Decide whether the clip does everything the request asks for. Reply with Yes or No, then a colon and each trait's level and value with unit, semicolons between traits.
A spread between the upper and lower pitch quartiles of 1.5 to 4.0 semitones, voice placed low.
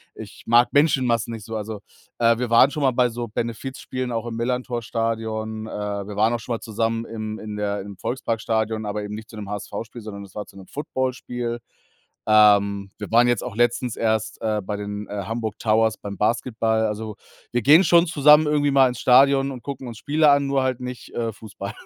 Yes: narrow, 2.6 semitones; low, 115 Hz